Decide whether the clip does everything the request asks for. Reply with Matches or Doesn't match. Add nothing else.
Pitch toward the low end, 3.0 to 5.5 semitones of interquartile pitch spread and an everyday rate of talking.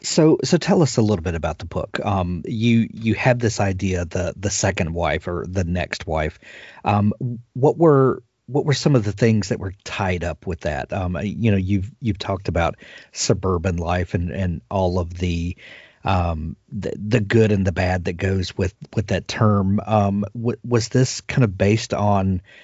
Matches